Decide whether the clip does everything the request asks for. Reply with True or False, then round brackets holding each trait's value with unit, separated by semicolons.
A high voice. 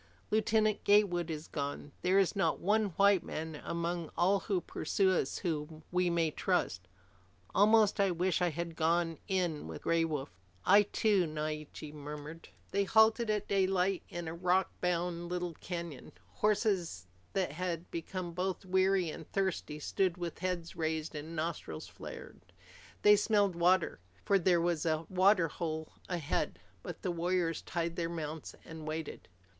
False (175 Hz)